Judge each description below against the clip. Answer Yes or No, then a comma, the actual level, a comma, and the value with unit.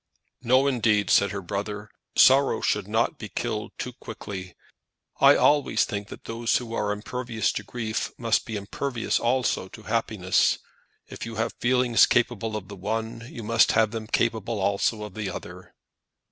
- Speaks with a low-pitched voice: Yes, low, 110 Hz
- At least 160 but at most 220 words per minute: Yes, average, 165 wpm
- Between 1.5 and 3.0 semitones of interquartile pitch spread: Yes, narrow, 2.4 semitones